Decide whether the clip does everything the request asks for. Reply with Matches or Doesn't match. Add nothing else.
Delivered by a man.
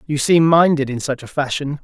Matches